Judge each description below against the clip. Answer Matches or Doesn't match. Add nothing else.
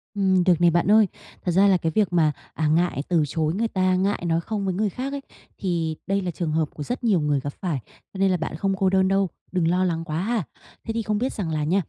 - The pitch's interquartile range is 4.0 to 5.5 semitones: Doesn't match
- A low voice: Doesn't match